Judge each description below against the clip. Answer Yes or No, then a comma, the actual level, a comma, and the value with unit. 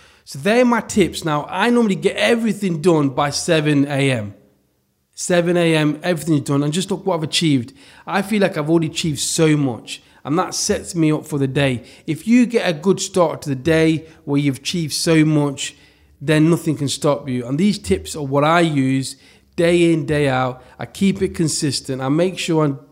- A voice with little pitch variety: No, average, 3.9 semitones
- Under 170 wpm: No, average, 200 wpm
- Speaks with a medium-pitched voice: Yes, medium, 155 Hz